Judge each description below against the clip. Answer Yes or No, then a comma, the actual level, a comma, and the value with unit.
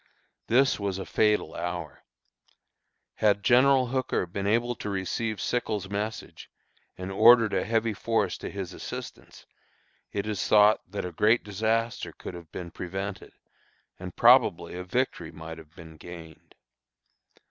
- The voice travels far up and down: No, average, 4.1 semitones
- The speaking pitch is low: Yes, low, 100 Hz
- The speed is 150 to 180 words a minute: No, average, 140 wpm